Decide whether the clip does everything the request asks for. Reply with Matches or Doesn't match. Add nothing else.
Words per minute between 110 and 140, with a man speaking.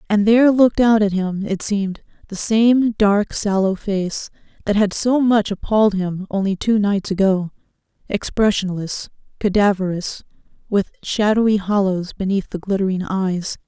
Doesn't match